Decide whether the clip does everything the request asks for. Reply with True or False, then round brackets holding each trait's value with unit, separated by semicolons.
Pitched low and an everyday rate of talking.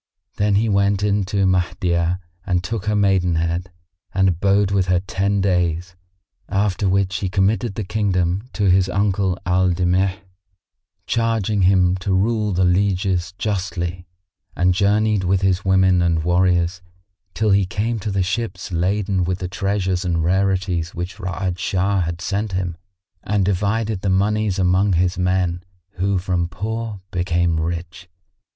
True (95 Hz; 150 wpm)